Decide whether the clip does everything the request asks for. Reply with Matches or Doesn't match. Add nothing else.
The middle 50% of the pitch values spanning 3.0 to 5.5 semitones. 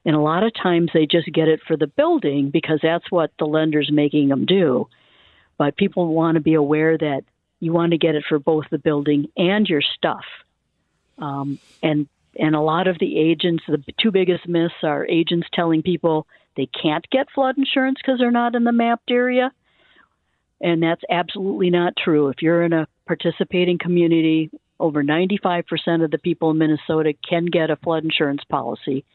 Doesn't match